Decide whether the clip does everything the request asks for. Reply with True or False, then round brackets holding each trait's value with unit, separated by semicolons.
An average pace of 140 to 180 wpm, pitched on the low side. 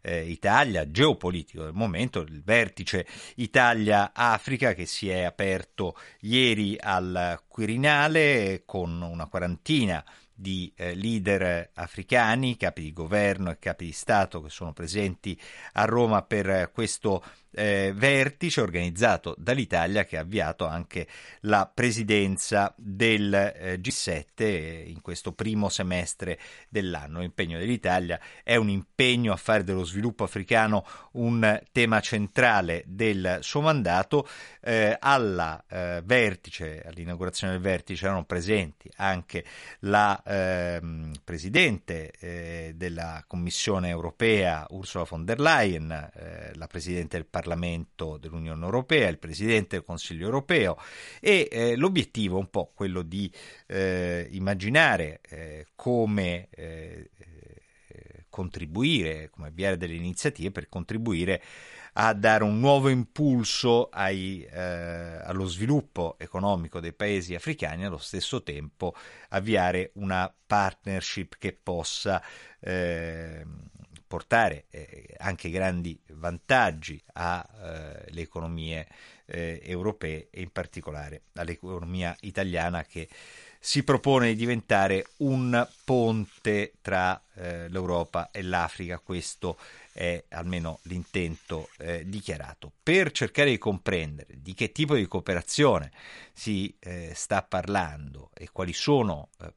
False (115 wpm; 95 Hz)